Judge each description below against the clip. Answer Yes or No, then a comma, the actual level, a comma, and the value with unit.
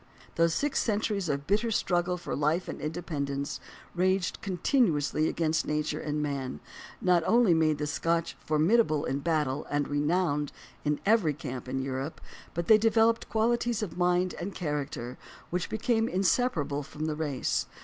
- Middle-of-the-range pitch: Yes, medium, 165 Hz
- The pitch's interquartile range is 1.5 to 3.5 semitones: No, average, 5.0 semitones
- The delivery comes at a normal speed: Yes, average, 160 wpm